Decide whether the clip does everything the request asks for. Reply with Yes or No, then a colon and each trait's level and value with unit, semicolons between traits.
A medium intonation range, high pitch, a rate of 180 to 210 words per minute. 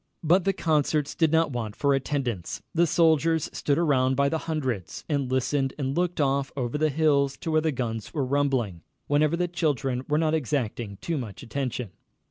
No: average, 3.6 semitones; medium, 140 Hz; average, 185 wpm